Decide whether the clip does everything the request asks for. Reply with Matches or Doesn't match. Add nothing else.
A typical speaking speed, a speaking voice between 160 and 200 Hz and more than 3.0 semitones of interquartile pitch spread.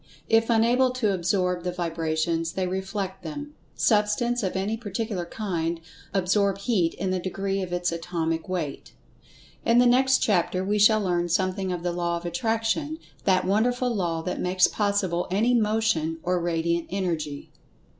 Matches